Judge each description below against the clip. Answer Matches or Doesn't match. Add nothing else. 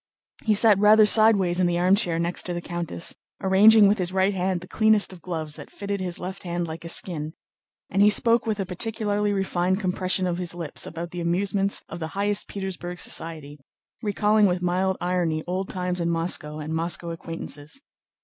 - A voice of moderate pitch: Matches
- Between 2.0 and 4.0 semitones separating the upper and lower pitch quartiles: Matches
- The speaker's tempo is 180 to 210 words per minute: Matches